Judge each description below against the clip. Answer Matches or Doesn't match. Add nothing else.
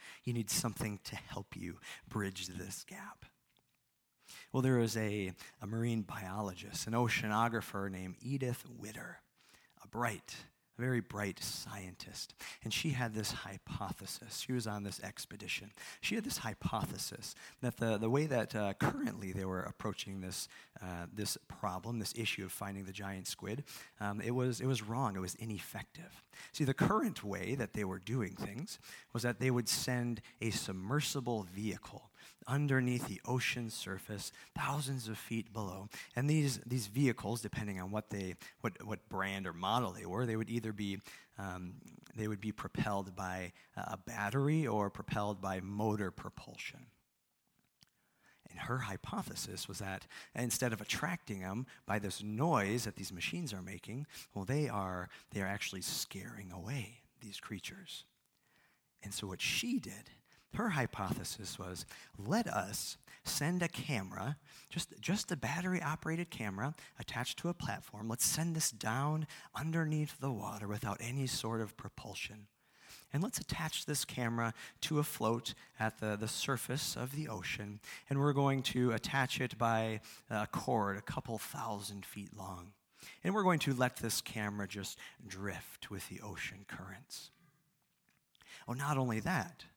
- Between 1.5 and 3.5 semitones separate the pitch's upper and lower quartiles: Doesn't match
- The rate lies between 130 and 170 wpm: Matches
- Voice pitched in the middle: Doesn't match